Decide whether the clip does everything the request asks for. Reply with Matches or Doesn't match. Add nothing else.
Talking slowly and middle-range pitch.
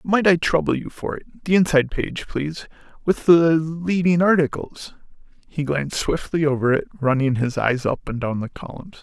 Doesn't match